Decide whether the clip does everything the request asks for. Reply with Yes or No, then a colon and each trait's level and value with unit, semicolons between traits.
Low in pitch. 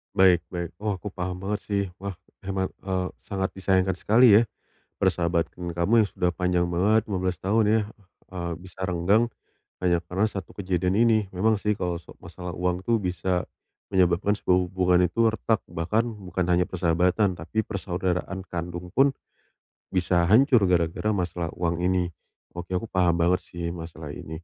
Yes: very low, 90 Hz